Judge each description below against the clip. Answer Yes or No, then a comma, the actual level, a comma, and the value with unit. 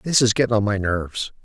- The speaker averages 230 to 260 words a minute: Yes, fast, 250 wpm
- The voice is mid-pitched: No, low, 110 Hz